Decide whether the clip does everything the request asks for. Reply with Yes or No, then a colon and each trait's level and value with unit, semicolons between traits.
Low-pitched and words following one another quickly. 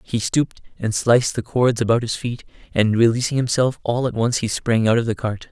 Yes: low, 115 Hz; fast, 230 wpm